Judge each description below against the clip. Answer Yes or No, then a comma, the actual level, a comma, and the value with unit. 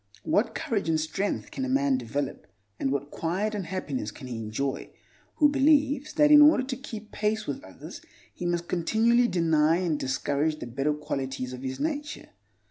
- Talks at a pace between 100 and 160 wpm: No, average, 180 wpm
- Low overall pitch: No, medium, 175 Hz